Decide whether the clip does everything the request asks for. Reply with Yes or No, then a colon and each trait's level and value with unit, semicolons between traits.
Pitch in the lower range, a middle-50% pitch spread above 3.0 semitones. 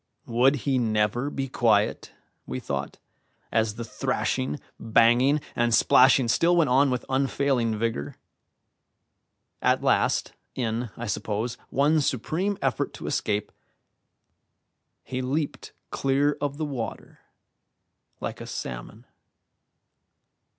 Yes: low, 125 Hz; average, 3.8 semitones